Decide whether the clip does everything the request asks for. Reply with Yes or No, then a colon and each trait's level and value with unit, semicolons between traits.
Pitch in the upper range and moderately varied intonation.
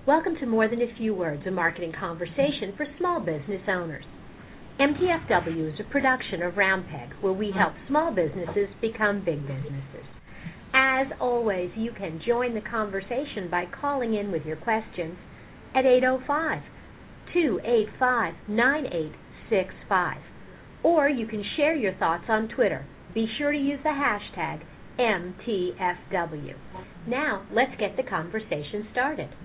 No: high, 220 Hz; wide, 6.6 semitones